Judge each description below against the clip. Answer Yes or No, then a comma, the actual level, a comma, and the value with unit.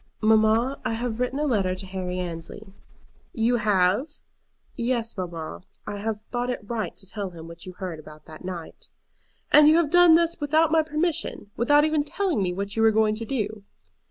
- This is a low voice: No, high, 220 Hz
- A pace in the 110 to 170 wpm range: No, average, 195 wpm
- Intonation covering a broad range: Yes, wide, 7.2 semitones